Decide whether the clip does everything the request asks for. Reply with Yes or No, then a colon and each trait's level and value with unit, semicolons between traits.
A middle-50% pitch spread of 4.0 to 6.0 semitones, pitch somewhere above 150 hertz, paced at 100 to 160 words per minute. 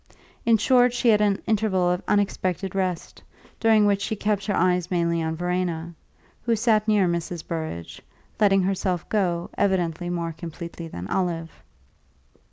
No: average, 3.4 semitones; medium, 185 Hz; average, 150 wpm